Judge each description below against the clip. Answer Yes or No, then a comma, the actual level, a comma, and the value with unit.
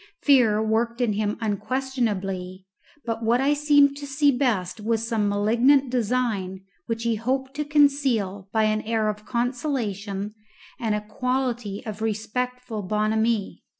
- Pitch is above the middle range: Yes, high, 225 Hz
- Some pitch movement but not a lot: Yes, average, 3.3 semitones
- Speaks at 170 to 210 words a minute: No, average, 140 wpm